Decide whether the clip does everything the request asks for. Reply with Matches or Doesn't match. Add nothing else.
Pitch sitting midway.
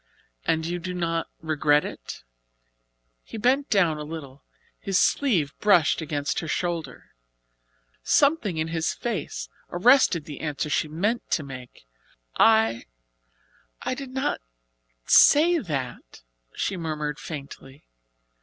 Matches